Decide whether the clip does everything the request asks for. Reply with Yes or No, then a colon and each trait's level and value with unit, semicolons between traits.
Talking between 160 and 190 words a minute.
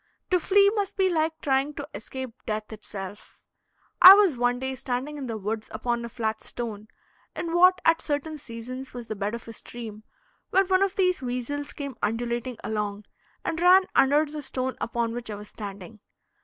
Yes: average, 185 wpm